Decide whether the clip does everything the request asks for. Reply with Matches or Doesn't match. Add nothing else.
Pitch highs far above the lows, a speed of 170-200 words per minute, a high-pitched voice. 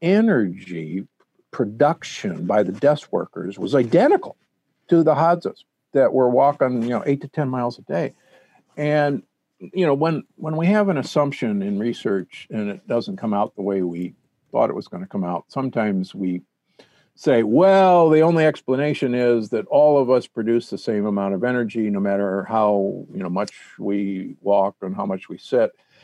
Doesn't match